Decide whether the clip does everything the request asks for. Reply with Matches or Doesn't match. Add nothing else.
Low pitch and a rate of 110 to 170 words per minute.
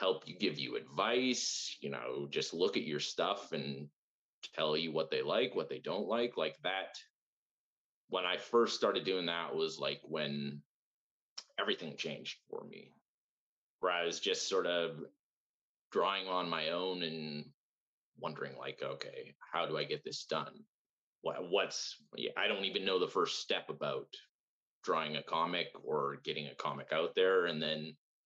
Matches